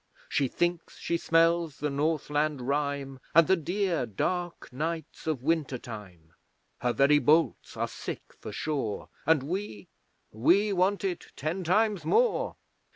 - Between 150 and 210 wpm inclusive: No, average, 140 wpm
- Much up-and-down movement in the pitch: No, average, 4.1 semitones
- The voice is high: No, medium, 155 Hz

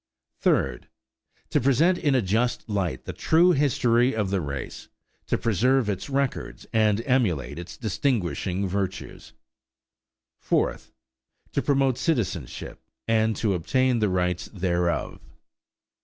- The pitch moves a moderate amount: No, wide, 6.3 semitones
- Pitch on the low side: Yes, low, 110 Hz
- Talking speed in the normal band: No, slow, 120 wpm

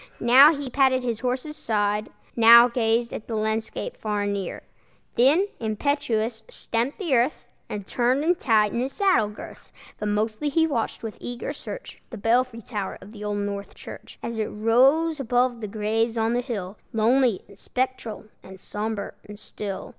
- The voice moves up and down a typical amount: Yes, average, 3.4 semitones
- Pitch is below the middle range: No, high, 230 Hz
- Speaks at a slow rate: No, average, 170 wpm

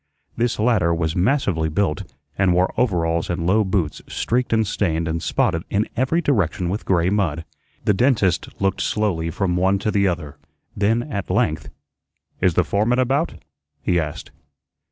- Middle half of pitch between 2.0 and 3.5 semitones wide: No, average, 4.5 semitones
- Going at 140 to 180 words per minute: Yes, average, 160 wpm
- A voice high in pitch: No, very low, 95 Hz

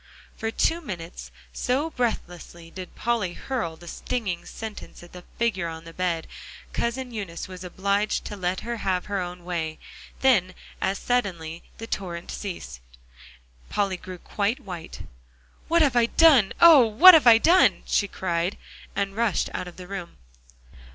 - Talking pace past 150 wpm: Yes, average, 160 wpm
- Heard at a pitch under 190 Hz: No, high, 195 Hz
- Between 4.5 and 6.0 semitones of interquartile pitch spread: Yes, average, 5.0 semitones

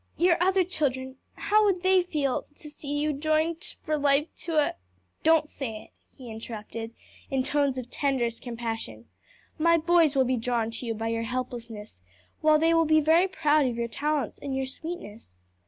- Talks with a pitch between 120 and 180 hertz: No, very high, 280 Hz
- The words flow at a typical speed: Yes, average, 185 wpm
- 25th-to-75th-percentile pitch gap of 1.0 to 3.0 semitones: No, average, 5.2 semitones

